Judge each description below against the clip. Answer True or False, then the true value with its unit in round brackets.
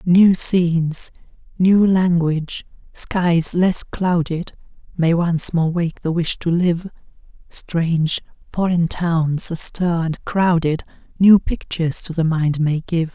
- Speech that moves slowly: True (130 wpm)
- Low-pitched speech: False (170 Hz)